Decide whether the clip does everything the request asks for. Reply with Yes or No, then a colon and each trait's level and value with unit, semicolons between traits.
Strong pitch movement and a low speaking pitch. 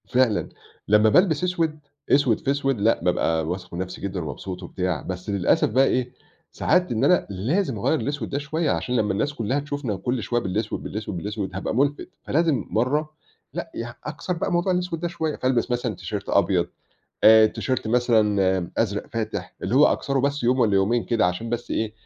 Yes: wide, 5.9 semitones; low, 120 Hz